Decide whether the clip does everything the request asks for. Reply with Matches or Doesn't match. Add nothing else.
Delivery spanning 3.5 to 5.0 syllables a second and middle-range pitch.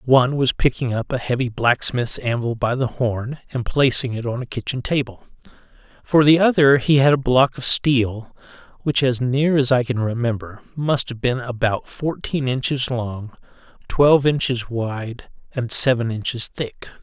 Doesn't match